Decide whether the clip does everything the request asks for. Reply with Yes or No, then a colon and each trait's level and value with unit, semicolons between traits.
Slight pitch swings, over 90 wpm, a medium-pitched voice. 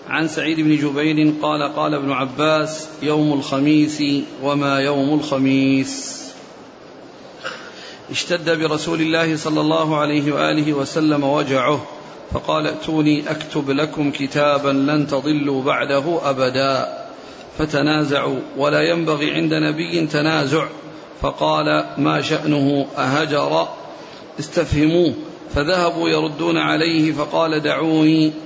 Yes: narrow, 1.9 semitones; average, 100 wpm; medium, 150 Hz